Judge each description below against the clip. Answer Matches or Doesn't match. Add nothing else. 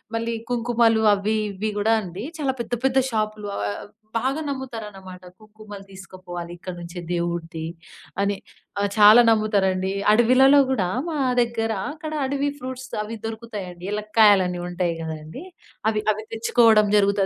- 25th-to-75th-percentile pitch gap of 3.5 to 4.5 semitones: Matches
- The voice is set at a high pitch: Matches